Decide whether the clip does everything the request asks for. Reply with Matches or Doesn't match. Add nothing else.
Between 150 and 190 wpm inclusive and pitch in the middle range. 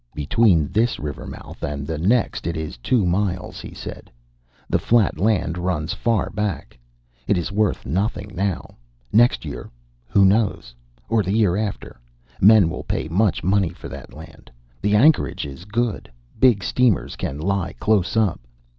Doesn't match